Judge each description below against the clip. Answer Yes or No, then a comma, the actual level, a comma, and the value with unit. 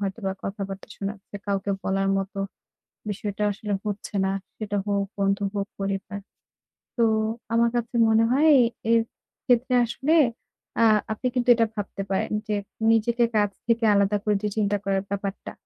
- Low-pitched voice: No, high, 205 Hz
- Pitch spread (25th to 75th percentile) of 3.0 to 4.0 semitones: No, narrow, 2.5 semitones